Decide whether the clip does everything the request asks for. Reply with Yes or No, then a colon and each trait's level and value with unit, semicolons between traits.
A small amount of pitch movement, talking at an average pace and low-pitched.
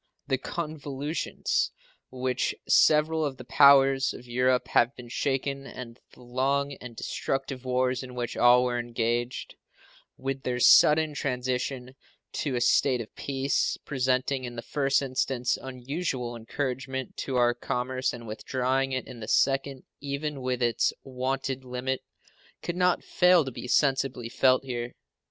Yes: narrow, 1.7 semitones; average, 145 wpm; low, 130 Hz